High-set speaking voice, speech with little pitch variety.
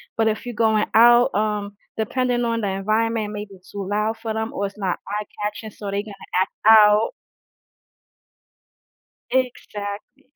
Yes: high, 215 Hz; narrow, 1.9 semitones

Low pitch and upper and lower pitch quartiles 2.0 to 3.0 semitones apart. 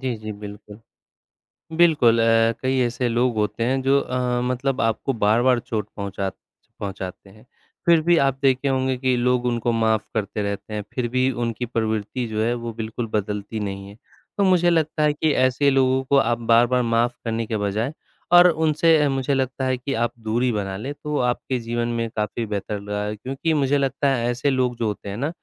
No: low, 120 Hz; average, 3.4 semitones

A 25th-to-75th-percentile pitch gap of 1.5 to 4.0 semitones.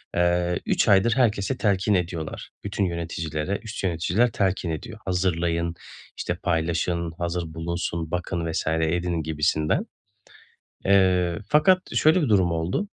Yes: average, 2.9 semitones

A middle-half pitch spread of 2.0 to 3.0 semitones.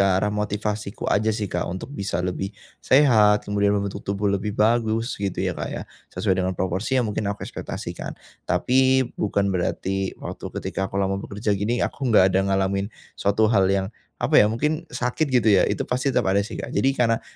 Yes: narrow, 2.6 semitones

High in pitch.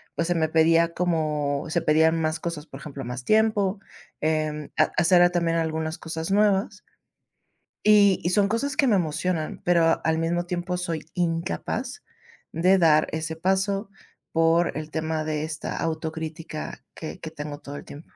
No: medium, 165 Hz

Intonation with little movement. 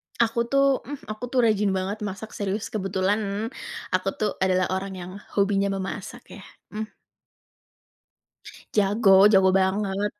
Yes: narrow, 2.2 semitones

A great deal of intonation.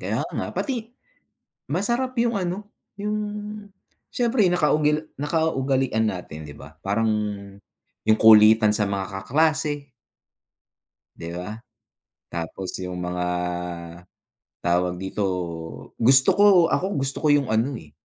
Yes: wide, 8.9 semitones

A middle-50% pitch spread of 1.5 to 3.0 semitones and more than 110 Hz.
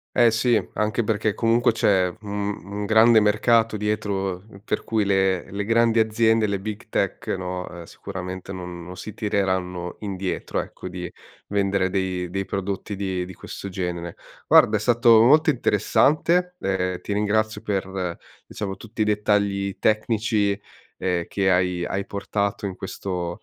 No: average, 2.7 semitones; low, 100 Hz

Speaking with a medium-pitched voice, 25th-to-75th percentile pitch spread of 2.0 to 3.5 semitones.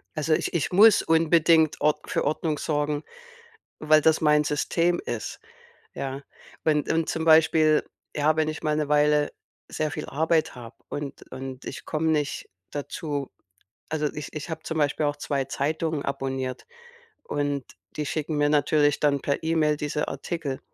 No: medium, 150 Hz; narrow, 1.6 semitones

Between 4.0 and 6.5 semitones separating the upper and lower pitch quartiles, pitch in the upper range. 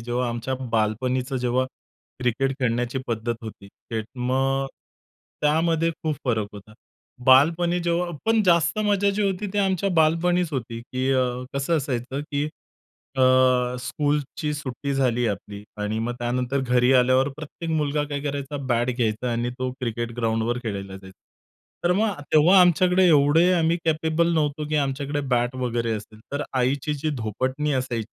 No: average, 4.6 semitones; low, 135 Hz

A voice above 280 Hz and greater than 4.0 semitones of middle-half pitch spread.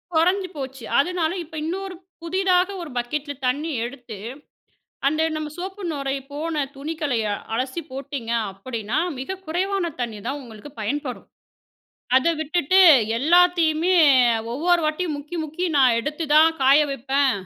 Yes: very high, 300 Hz; average, 4.6 semitones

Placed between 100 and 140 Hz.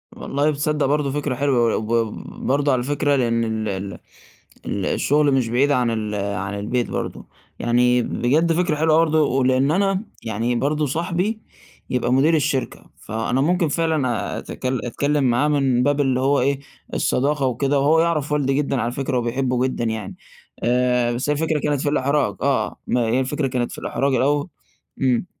Yes: low, 135 Hz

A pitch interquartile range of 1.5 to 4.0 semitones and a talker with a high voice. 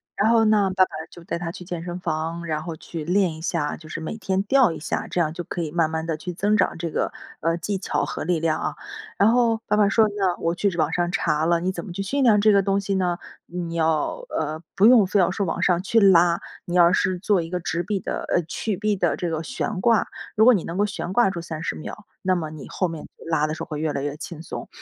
No: average, 3.4 semitones; medium, 175 Hz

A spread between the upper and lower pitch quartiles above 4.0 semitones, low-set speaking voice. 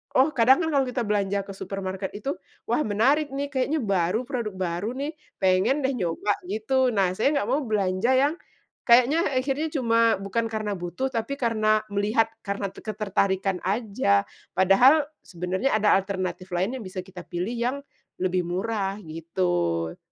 No: average, 5.1 semitones; high, 210 Hz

